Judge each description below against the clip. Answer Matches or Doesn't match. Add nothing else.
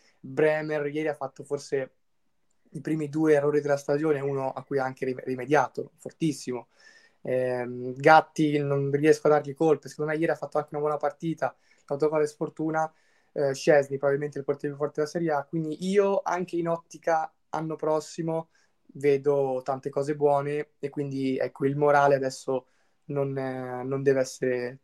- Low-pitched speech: Doesn't match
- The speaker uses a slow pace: Doesn't match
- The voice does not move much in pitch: Matches